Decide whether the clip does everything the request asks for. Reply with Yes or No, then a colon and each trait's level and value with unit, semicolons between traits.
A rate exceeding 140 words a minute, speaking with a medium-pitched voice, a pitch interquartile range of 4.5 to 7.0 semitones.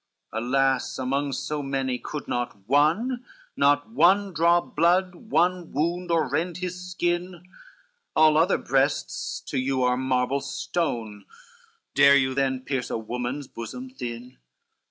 No: slow, 135 wpm; medium, 145 Hz; average, 5.2 semitones